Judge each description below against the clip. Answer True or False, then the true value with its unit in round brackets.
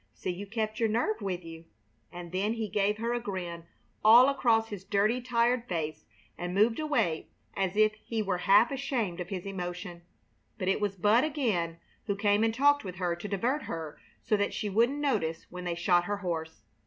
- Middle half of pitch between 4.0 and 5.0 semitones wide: True (4.3 semitones)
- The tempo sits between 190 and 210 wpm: True (200 wpm)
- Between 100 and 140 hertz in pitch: False (205 Hz)